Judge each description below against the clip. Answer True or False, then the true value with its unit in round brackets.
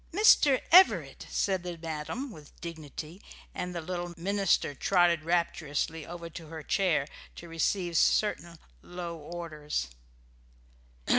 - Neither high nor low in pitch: True (170 Hz)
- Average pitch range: False (2.2 semitones)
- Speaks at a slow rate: True (120 wpm)